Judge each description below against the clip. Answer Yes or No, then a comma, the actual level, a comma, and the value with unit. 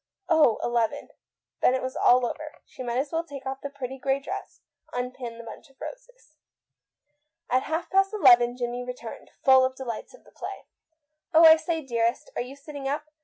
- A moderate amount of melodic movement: Yes, average, 3.8 semitones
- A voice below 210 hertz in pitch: No, very high, 265 Hz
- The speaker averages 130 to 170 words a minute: No, average, 195 wpm